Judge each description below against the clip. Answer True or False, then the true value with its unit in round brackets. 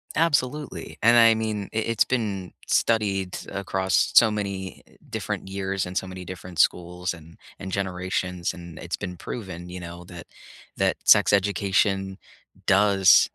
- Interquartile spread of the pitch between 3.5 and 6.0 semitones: False (2.4 semitones)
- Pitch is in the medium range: False (95 Hz)